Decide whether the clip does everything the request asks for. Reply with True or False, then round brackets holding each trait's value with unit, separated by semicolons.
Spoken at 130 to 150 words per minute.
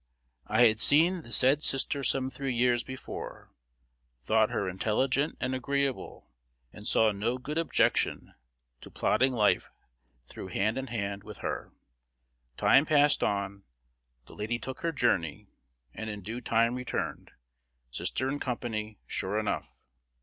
True (140 wpm)